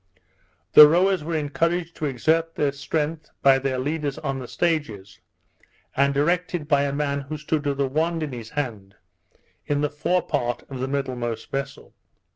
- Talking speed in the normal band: Yes, average, 165 wpm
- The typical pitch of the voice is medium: Yes, medium, 145 Hz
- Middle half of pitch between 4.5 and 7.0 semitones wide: No, average, 2.8 semitones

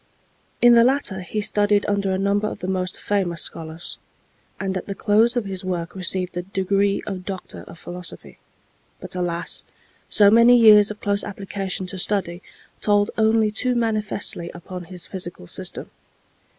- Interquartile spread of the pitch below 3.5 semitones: Yes, narrow, 2.5 semitones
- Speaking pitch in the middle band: No, high, 195 Hz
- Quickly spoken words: No, average, 165 wpm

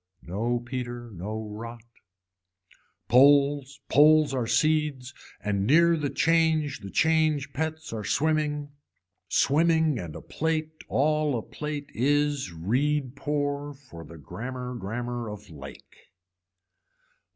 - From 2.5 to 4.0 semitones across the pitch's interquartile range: No, average, 4.6 semitones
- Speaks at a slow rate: Yes, slow, 115 wpm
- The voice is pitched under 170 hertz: Yes, medium, 140 Hz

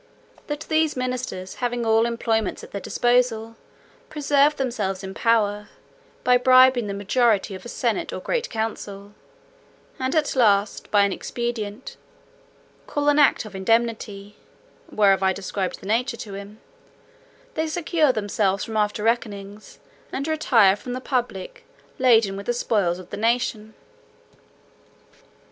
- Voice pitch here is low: No, high, 225 Hz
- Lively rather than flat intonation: No, average, 3.8 semitones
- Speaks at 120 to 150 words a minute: Yes, average, 140 wpm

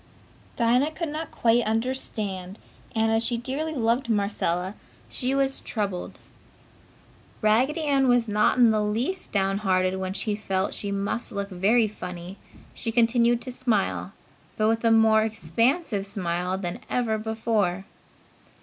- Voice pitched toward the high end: Yes, high, 220 Hz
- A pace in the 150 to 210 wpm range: No, average, 140 wpm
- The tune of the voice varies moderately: Yes, average, 3.6 semitones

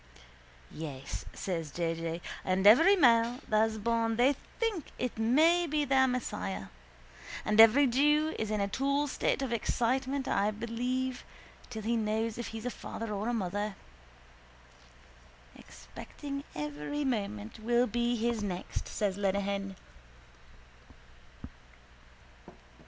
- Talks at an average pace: No, slow, 125 wpm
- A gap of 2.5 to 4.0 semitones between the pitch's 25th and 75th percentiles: No, average, 4.4 semitones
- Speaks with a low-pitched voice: No, high, 230 Hz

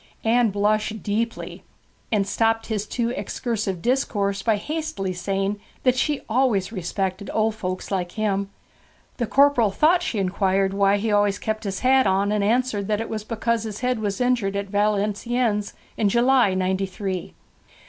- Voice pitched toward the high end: Yes, high, 210 Hz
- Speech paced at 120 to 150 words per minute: No, average, 160 wpm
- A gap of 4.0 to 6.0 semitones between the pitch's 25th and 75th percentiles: No, average, 2.9 semitones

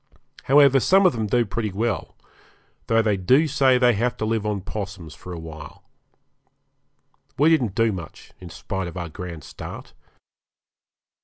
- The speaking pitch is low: Yes, low, 110 Hz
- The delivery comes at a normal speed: Yes, average, 160 wpm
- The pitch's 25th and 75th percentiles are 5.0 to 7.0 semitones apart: Yes, wide, 5.4 semitones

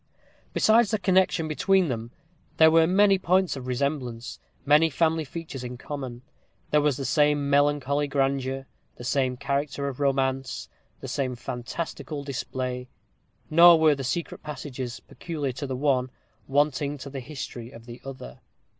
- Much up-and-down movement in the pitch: No, average, 3.1 semitones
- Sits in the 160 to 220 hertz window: No, medium, 140 Hz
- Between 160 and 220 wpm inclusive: No, average, 150 wpm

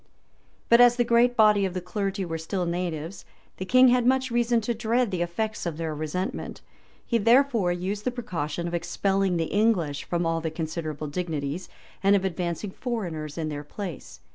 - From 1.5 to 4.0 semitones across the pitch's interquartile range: No, wide, 5.5 semitones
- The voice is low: No, medium, 185 Hz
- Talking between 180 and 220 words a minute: Yes, average, 185 wpm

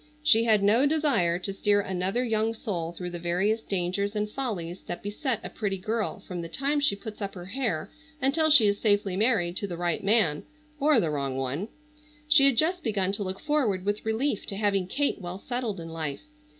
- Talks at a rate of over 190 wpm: Yes, average, 200 wpm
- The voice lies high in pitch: Yes, high, 205 Hz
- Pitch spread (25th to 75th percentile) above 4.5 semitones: Yes, average, 5.1 semitones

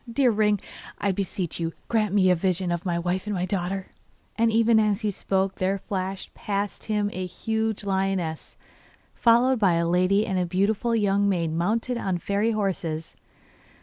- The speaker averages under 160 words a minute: No, average, 175 wpm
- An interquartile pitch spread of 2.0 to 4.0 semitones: Yes, average, 2.8 semitones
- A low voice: No, high, 195 Hz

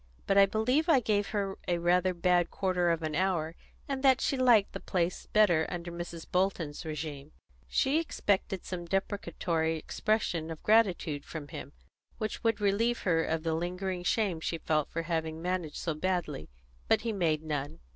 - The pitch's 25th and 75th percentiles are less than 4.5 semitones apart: Yes, average, 4.0 semitones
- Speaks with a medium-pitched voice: Yes, medium, 180 Hz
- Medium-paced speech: Yes, average, 175 wpm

